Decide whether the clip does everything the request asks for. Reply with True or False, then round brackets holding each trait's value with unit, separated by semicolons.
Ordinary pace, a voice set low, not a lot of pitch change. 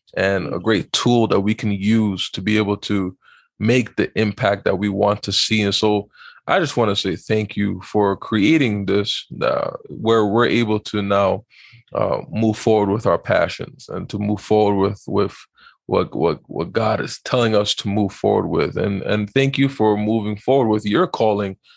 True (195 wpm; 105 Hz; 1.6 semitones)